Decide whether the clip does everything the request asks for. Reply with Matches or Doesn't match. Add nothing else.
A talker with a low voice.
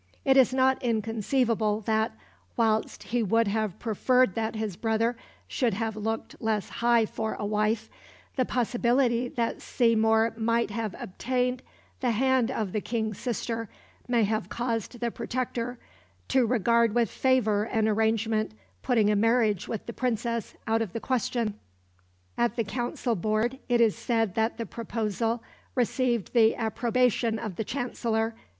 Doesn't match